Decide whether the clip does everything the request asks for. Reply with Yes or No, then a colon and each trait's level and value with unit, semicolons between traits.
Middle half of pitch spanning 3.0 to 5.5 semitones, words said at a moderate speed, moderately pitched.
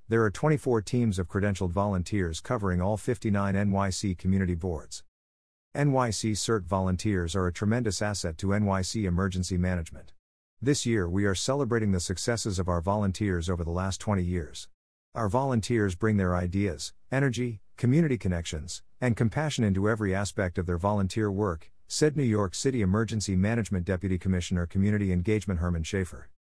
No: average, 3.5 semitones; average, 155 wpm; low, 100 Hz